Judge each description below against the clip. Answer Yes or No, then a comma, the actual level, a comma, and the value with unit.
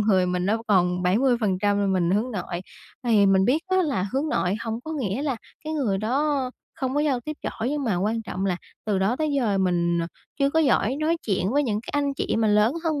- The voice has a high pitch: Yes, high, 225 Hz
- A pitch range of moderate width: No, wide, 6.3 semitones